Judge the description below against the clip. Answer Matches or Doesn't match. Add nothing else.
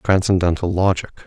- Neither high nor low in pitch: Doesn't match